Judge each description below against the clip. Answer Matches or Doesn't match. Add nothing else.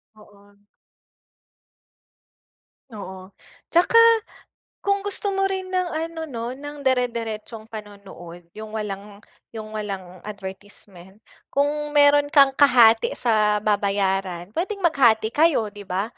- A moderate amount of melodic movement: Doesn't match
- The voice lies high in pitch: Matches